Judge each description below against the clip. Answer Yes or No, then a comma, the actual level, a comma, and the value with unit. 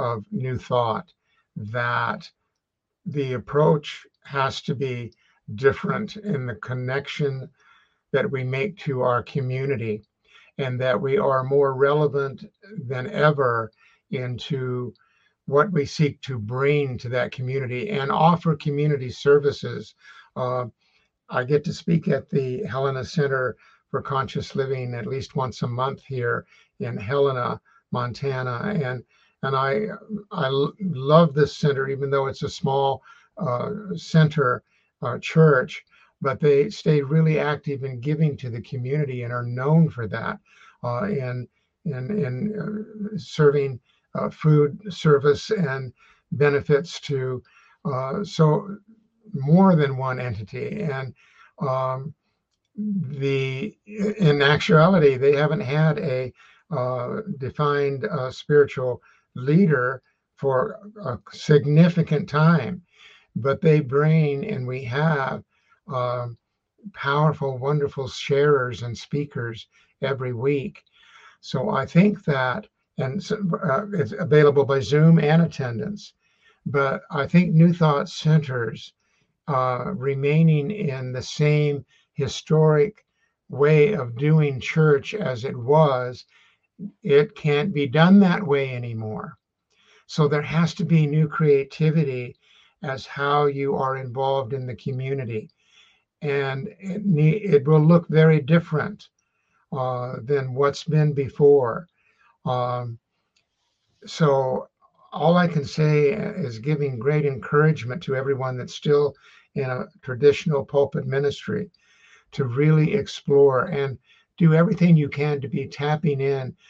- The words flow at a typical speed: No, slow, 125 wpm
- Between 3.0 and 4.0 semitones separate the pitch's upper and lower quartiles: Yes, average, 3.4 semitones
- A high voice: No, medium, 145 Hz